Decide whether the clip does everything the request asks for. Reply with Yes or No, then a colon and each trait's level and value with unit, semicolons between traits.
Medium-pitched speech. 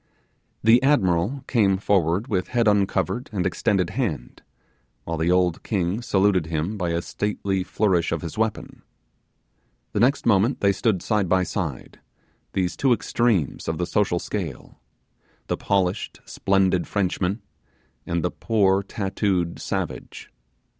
No: very low, 95 Hz